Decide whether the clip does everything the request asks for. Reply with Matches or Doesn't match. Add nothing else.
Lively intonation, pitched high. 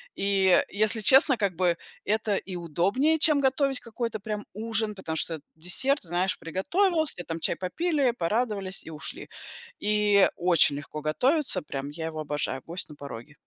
Matches